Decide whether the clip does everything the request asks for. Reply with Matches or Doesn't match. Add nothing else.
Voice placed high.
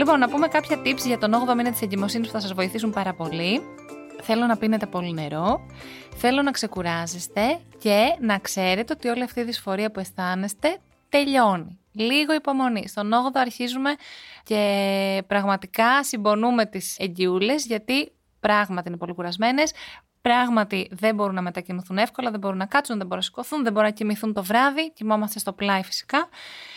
Matches